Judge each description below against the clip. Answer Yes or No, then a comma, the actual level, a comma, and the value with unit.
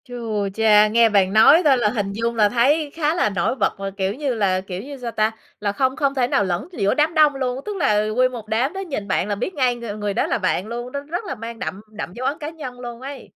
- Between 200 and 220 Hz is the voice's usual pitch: No, high, 235 Hz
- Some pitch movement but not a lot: Yes, average, 4.8 semitones